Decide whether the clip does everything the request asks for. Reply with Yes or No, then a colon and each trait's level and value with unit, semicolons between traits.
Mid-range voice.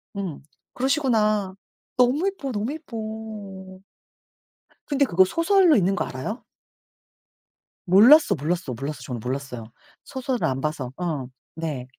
No: high, 195 Hz